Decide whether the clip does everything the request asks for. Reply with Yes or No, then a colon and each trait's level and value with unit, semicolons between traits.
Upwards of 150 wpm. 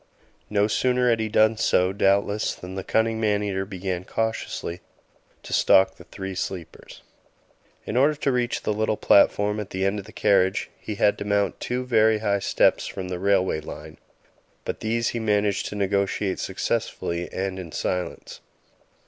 Yes: average, 170 wpm